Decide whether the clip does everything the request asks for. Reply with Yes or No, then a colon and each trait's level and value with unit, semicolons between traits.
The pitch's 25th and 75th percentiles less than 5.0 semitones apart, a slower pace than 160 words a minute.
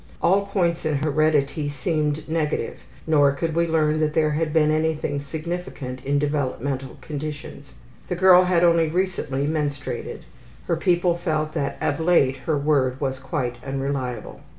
Yes: average, 2.7 semitones; average, 150 wpm